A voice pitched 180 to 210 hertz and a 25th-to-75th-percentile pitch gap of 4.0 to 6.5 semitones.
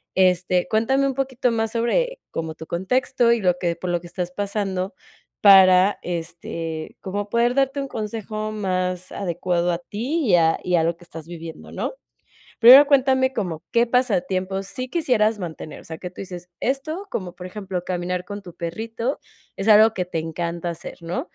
Yes: high, 190 Hz; average, 4.9 semitones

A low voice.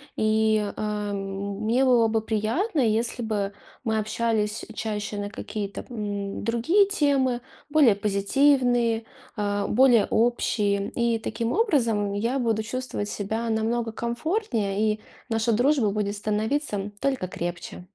No: high, 220 Hz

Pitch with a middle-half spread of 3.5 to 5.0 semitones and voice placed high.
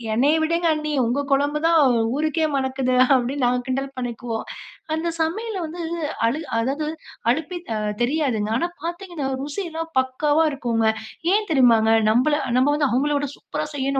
Yes: average, 4.0 semitones; very high, 285 Hz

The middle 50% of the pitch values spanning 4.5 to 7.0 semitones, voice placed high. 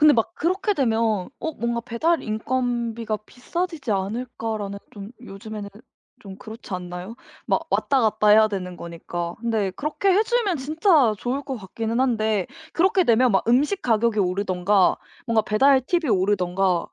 Yes: average, 5.1 semitones; high, 225 Hz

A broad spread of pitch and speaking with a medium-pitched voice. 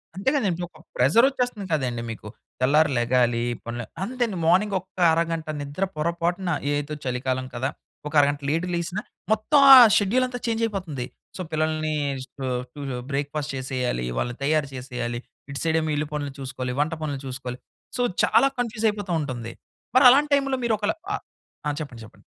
Yes: wide, 7.4 semitones; medium, 155 Hz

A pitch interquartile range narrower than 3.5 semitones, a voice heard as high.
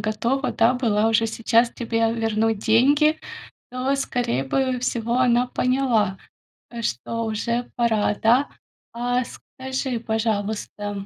Yes: narrow, 2.4 semitones; high, 230 Hz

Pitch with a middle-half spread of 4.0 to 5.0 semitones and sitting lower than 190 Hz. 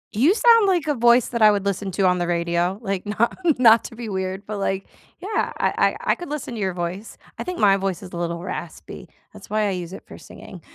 No: average, 4.6 semitones; high, 200 Hz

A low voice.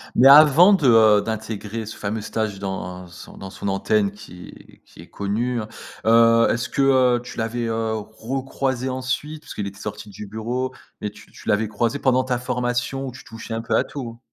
Yes: low, 115 Hz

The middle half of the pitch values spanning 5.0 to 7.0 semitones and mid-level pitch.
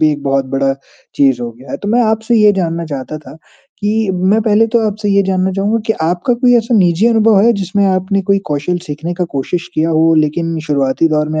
Yes: wide, 5.5 semitones; medium, 180 Hz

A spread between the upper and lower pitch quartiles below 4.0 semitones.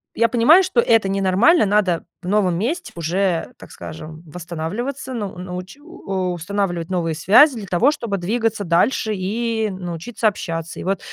No: average, 4.6 semitones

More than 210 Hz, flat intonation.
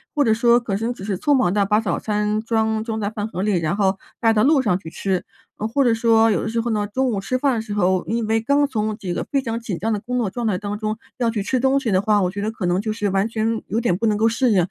Yes: high, 220 Hz; narrow, 2.3 semitones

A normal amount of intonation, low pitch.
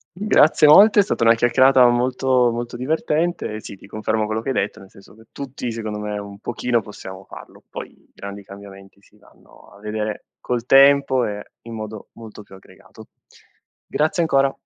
Yes: average, 4.2 semitones; low, 115 Hz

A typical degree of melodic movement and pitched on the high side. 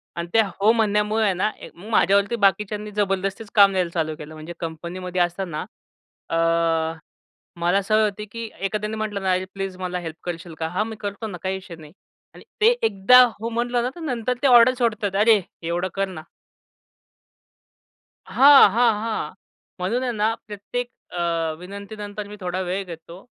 Yes: average, 3.4 semitones; high, 200 Hz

